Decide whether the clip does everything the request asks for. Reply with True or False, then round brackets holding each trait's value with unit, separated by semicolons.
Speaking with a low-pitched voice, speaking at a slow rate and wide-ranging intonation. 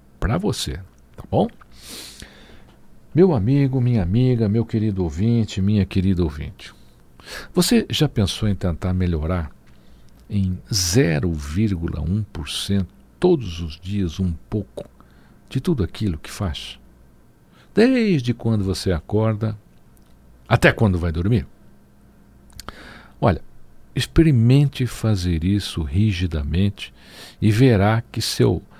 True (100 Hz; 100 wpm; 5.8 semitones)